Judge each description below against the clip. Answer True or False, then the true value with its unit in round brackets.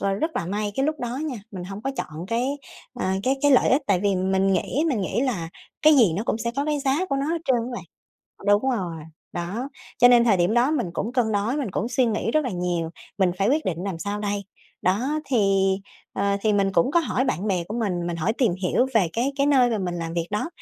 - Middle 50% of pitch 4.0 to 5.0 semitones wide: False (5.4 semitones)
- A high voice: True (215 Hz)